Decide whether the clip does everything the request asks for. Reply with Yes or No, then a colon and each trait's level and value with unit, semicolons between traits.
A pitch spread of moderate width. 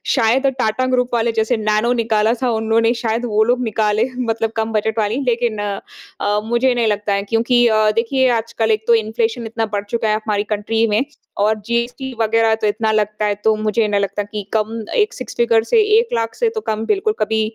No: narrow, 1.7 semitones